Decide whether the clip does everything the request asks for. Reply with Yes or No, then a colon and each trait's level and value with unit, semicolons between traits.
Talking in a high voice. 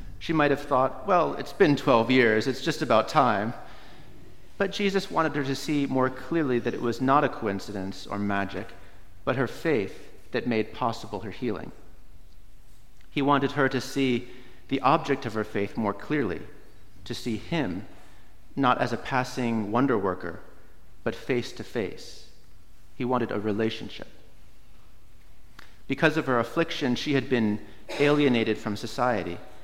No: low, 120 Hz